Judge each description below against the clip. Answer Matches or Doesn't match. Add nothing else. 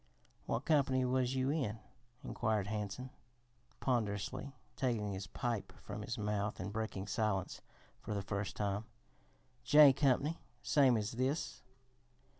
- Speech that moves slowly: Matches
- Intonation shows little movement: Doesn't match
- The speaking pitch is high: Doesn't match